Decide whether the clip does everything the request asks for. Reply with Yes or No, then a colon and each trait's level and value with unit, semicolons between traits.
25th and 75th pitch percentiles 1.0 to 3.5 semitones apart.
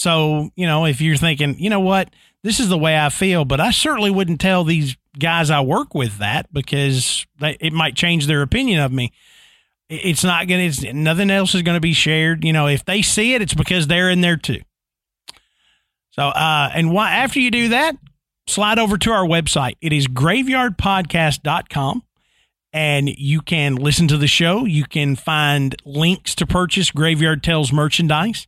No: average, 4.1 semitones